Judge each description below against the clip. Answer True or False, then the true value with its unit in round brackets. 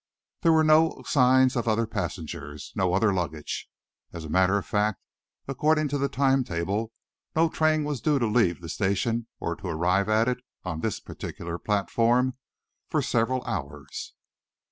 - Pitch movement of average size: False (6.3 semitones)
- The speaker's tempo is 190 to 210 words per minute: False (165 wpm)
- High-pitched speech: False (110 Hz)